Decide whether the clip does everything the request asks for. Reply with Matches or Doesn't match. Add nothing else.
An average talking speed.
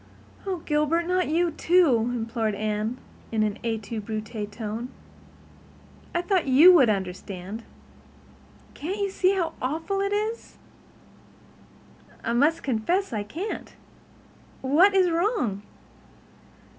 Doesn't match